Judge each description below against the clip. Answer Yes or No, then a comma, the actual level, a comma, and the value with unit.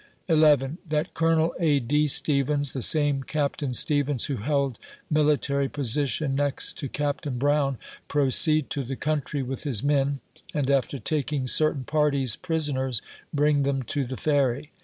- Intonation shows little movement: Yes, narrow, 1.9 semitones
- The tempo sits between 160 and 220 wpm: No, average, 145 wpm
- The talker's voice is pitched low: No, medium, 145 Hz